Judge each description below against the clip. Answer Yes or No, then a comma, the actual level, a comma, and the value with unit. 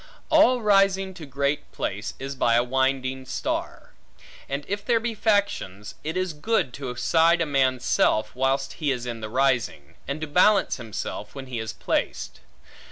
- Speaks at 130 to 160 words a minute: No, average, 170 wpm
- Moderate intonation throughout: No, wide, 6.7 semitones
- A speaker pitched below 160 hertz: Yes, medium, 140 Hz